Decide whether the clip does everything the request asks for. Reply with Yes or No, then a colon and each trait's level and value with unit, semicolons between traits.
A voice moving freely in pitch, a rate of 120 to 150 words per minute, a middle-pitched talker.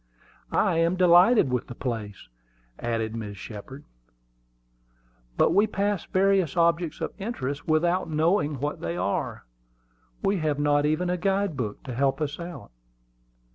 Yes: wide, 6.0 semitones; average, 140 wpm; medium, 155 Hz